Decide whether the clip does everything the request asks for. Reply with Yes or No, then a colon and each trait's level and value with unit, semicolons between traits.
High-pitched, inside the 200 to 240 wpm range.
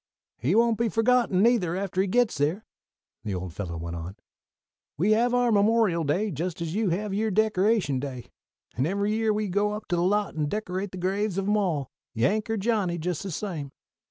Yes: high, 195 Hz; fast, 205 wpm